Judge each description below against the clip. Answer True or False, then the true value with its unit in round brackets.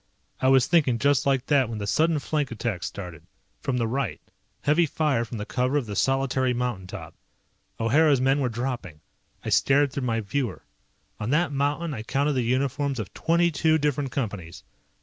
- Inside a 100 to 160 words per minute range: False (185 wpm)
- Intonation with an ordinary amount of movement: True (3.8 semitones)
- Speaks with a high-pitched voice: False (130 Hz)